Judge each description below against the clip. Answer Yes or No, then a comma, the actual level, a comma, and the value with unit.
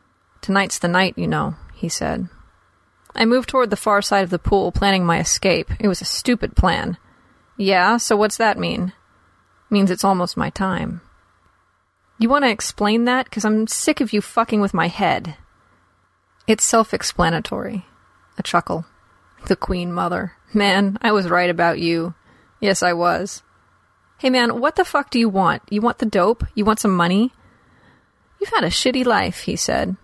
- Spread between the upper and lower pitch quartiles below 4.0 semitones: No, average, 4.6 semitones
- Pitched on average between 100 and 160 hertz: No, high, 200 Hz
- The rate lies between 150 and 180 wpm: Yes, average, 170 wpm